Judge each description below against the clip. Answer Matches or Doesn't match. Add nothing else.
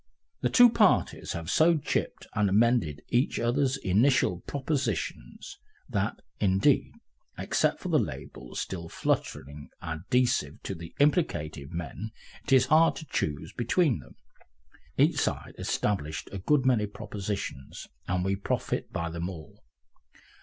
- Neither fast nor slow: Doesn't match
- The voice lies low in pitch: Matches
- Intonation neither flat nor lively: Doesn't match